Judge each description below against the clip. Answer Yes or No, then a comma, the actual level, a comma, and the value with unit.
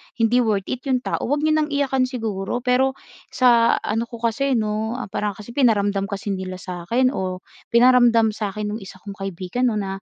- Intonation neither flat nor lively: Yes, average, 4.0 semitones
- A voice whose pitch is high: Yes, high, 225 Hz